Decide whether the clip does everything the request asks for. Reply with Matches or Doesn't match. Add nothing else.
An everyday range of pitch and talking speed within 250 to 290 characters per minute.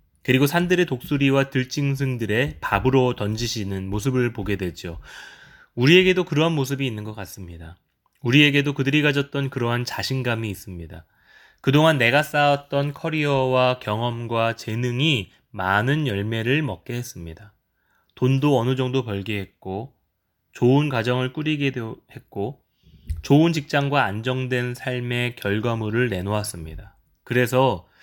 Doesn't match